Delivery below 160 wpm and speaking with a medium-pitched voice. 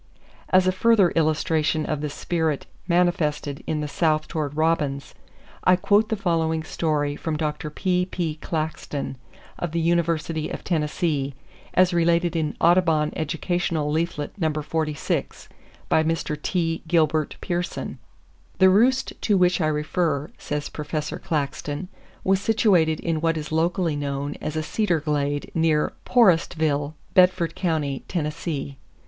Yes: slow, 135 wpm; medium, 160 Hz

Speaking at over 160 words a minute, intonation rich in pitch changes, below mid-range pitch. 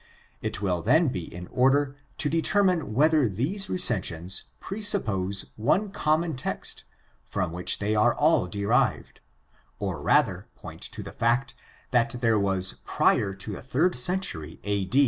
No: average, 145 wpm; wide, 8.2 semitones; low, 115 Hz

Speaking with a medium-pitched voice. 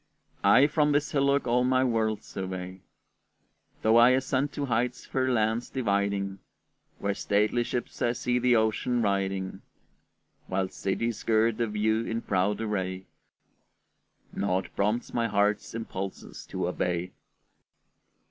No: low, 110 Hz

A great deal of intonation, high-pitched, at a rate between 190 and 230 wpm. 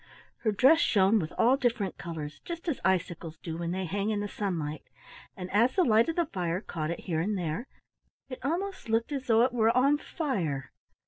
Yes: wide, 6.7 semitones; high, 210 Hz; fast, 205 wpm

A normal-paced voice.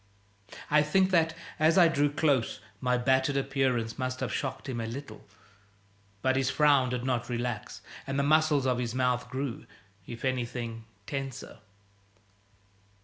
Yes: average, 145 wpm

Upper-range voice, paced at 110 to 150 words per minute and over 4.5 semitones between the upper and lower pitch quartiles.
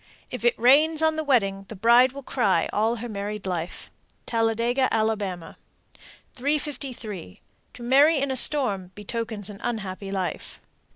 Yes: high, 230 Hz; average, 140 wpm; average, 4.9 semitones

